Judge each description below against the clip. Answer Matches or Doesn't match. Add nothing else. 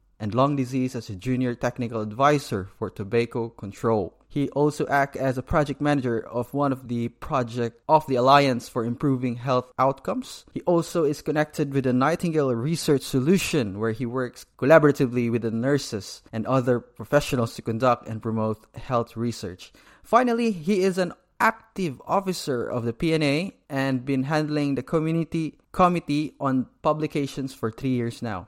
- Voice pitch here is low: Matches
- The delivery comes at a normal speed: Matches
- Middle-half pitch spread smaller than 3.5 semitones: Doesn't match